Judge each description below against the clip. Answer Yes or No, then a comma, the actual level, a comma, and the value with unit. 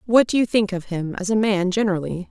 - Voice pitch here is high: Yes, high, 200 Hz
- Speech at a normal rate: No, fast, 260 wpm